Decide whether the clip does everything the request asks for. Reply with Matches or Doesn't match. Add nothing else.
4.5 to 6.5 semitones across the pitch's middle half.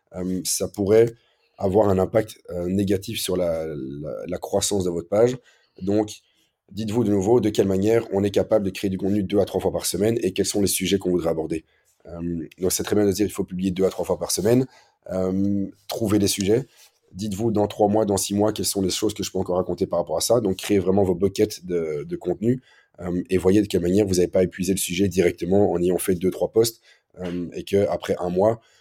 Doesn't match